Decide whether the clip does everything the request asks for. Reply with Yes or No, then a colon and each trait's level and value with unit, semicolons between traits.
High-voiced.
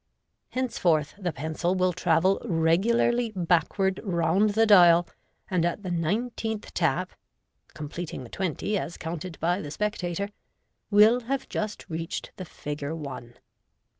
No: medium, 180 Hz